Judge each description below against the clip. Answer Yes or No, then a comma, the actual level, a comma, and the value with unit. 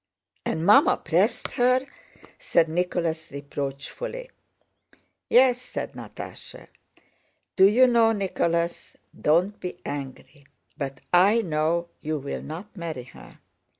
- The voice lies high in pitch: No, medium, 170 Hz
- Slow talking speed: Yes, slow, 100 wpm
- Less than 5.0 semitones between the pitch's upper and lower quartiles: No, wide, 5.4 semitones